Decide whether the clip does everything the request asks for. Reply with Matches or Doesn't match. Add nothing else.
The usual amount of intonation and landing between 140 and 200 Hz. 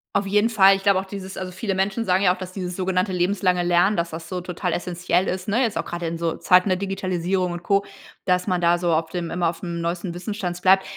Doesn't match